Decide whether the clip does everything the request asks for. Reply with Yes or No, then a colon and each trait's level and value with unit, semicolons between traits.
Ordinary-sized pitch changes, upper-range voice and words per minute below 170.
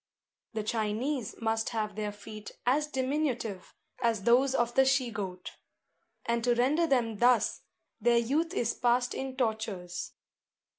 Yes: average, 3.3 semitones; high, 235 Hz; average, 140 wpm